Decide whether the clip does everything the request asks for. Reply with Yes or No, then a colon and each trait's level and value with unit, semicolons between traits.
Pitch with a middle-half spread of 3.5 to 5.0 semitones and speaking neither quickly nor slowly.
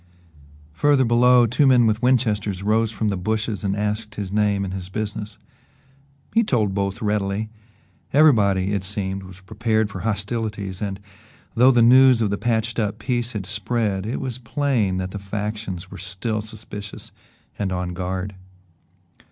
No: average, 2.9 semitones; average, 160 wpm